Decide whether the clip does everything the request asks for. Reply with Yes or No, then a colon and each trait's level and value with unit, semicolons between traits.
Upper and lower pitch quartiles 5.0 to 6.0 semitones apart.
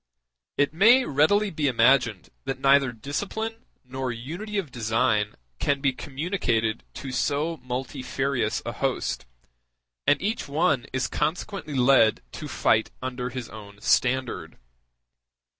No: average, 3.9 semitones